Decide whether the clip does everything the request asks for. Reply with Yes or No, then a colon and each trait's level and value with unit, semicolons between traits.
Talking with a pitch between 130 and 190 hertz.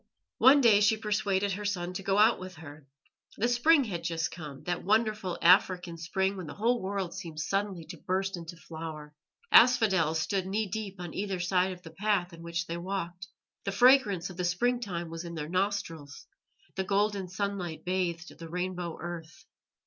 Yes: medium, 185 Hz